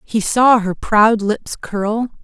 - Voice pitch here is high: Yes, high, 215 Hz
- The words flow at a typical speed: Yes, average, 160 wpm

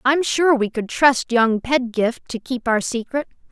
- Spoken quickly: No, average, 190 wpm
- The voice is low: No, very high, 250 Hz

